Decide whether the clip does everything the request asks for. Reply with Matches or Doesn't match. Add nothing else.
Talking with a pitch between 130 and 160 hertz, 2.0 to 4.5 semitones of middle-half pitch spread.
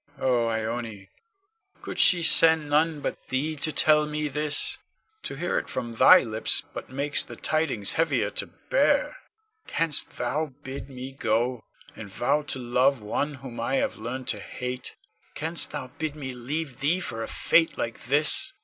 Matches